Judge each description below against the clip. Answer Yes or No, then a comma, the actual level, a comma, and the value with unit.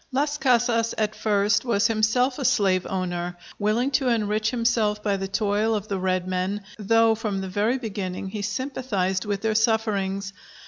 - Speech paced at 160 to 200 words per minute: Yes, average, 170 wpm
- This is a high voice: Yes, high, 210 Hz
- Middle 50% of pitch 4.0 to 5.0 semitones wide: No, average, 2.8 semitones